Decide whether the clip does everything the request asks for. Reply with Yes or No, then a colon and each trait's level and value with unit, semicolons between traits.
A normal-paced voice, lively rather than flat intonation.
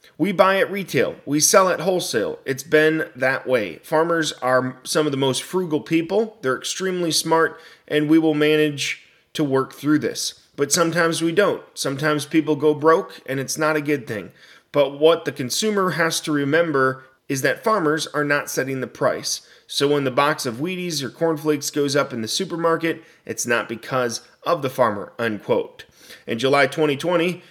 No: average, 185 wpm; average, 3.1 semitones